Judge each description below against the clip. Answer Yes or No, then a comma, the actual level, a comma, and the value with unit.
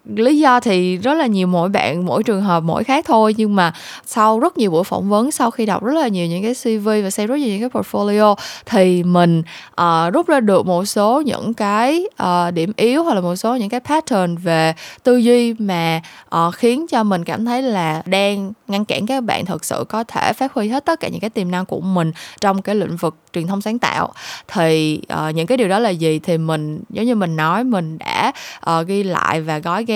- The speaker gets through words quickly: No, average, 240 wpm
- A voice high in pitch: Yes, high, 205 Hz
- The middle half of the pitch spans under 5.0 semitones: No, wide, 5.4 semitones